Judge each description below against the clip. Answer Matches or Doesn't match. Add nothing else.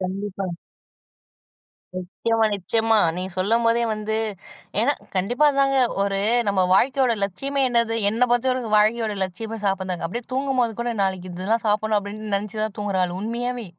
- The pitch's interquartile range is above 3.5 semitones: Doesn't match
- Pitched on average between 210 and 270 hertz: Matches